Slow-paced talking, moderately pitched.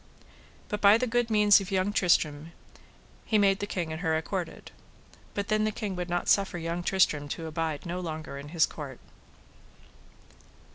No: average, 175 wpm; medium, 180 Hz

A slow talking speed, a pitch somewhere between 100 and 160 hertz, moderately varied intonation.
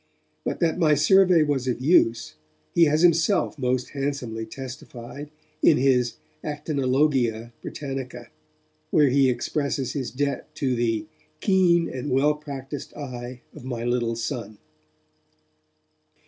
Yes: slow, 120 wpm; low, 135 Hz; average, 3.4 semitones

